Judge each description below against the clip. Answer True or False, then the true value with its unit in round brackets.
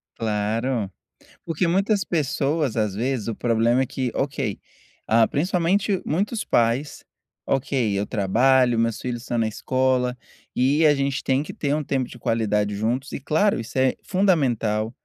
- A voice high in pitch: False (130 Hz)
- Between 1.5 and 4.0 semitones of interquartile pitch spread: False (4.4 semitones)